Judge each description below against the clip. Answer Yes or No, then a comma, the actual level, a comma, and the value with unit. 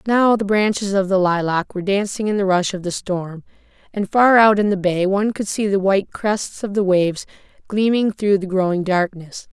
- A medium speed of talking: No, fast, 215 wpm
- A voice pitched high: Yes, high, 195 Hz